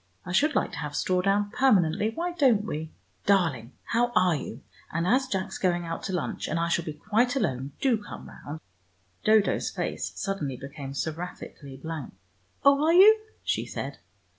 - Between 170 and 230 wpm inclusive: Yes, average, 180 wpm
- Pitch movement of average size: No, wide, 6.6 semitones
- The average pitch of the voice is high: No, medium, 180 Hz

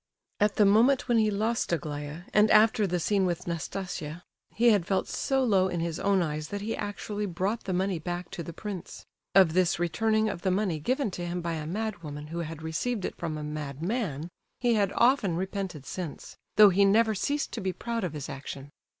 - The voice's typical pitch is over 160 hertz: Yes, medium, 185 Hz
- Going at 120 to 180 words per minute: No, fast, 205 wpm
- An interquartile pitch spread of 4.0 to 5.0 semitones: Yes, average, 4.4 semitones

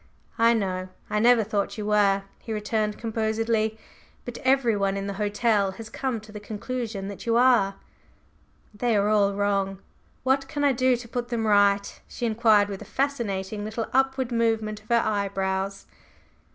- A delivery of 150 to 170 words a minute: Yes, average, 165 wpm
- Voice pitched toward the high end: Yes, high, 215 Hz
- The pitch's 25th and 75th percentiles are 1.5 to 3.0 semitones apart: Yes, average, 2.7 semitones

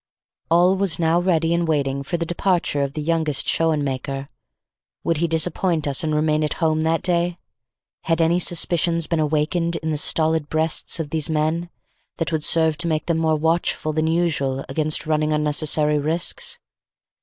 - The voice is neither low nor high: Yes, medium, 160 Hz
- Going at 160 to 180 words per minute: Yes, average, 170 wpm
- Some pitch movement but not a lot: No, narrow, 1.7 semitones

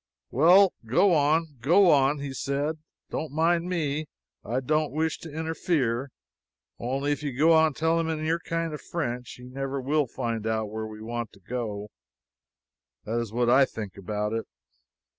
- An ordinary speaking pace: Yes, average, 180 wpm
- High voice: No, medium, 140 Hz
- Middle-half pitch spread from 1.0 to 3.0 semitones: No, average, 5.2 semitones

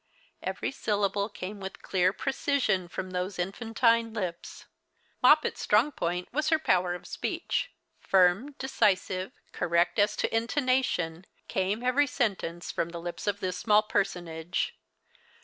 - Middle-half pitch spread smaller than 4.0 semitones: No, average, 4.4 semitones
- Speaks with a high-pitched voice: Yes, high, 200 Hz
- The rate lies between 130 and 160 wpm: Yes, slow, 135 wpm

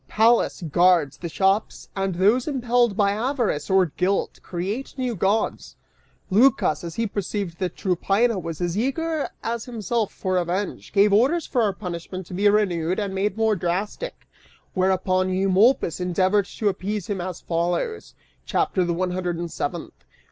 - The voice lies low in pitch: No, high, 195 Hz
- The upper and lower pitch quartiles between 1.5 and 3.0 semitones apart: No, average, 3.6 semitones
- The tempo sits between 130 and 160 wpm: Yes, average, 155 wpm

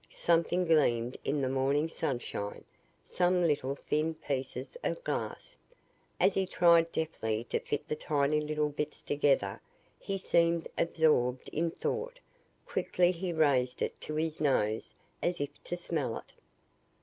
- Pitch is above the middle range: No, medium, 155 Hz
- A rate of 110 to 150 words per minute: Yes, average, 140 wpm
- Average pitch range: Yes, average, 3.7 semitones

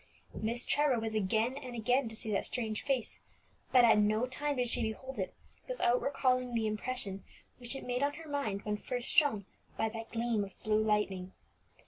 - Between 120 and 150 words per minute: No, average, 190 wpm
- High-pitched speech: Yes, high, 235 Hz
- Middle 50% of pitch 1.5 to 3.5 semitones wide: Yes, average, 3.0 semitones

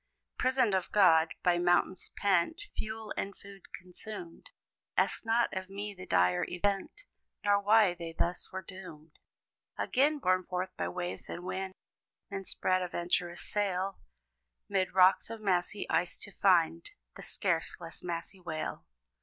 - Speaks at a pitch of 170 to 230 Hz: Yes, medium, 185 Hz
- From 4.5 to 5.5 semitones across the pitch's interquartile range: No, narrow, 2.4 semitones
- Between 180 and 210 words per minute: No, average, 145 wpm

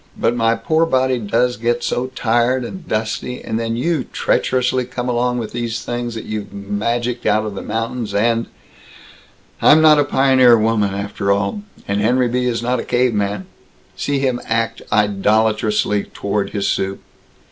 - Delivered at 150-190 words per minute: Yes, average, 165 wpm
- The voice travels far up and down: No, average, 2.8 semitones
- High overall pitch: No, low, 115 Hz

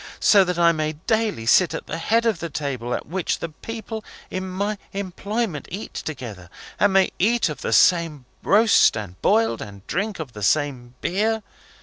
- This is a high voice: No, medium, 170 Hz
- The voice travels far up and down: Yes, wide, 6.8 semitones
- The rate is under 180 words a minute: No, average, 185 wpm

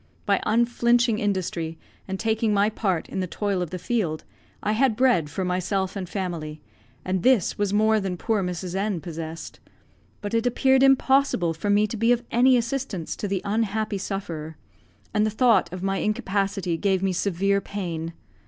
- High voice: Yes, high, 200 Hz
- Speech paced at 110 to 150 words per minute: No, average, 175 wpm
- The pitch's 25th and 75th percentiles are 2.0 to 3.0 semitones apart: No, average, 3.6 semitones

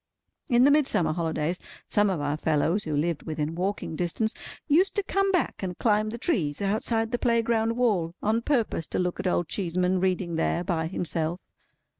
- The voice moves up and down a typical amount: No, wide, 5.7 semitones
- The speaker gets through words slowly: No, average, 180 wpm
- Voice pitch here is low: No, medium, 185 Hz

